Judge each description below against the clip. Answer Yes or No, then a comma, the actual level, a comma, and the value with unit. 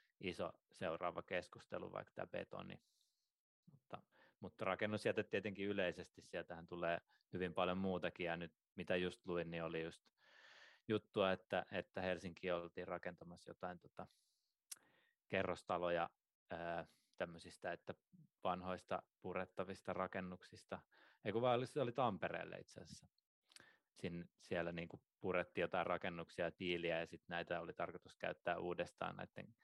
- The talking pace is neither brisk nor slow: Yes, average, 125 wpm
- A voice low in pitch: Yes, very low, 90 Hz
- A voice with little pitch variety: Yes, narrow, 1.5 semitones